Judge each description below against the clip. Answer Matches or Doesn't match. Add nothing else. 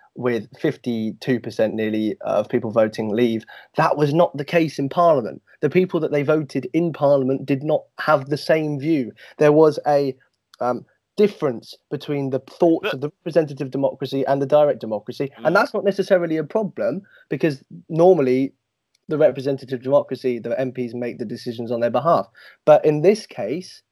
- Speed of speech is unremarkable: Matches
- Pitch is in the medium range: Matches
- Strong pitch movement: Doesn't match